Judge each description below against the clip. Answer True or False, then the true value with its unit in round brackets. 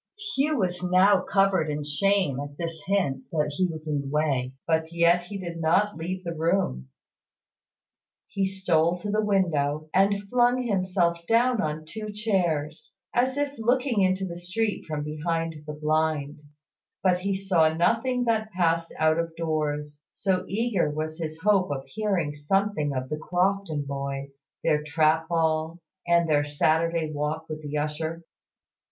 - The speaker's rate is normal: True (160 wpm)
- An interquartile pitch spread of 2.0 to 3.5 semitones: False (4.2 semitones)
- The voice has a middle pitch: True (165 Hz)